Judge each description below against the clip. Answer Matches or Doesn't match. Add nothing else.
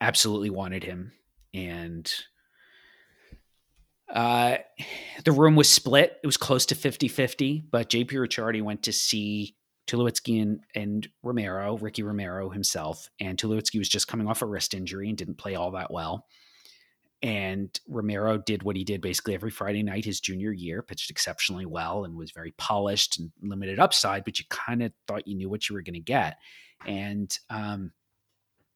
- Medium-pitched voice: Doesn't match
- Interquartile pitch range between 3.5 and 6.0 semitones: Doesn't match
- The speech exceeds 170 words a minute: Doesn't match